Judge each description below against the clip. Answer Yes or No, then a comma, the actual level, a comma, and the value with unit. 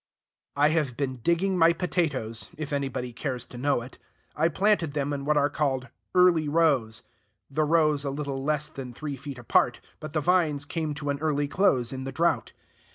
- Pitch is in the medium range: Yes, medium, 145 Hz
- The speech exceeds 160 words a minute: Yes, average, 190 wpm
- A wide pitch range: No, average, 2.8 semitones